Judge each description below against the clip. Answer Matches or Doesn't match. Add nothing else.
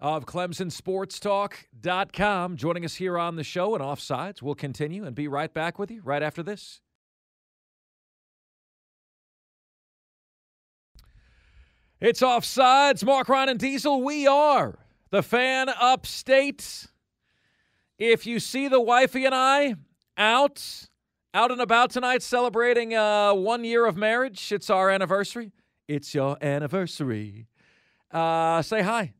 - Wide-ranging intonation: Matches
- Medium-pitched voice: Doesn't match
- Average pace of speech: Doesn't match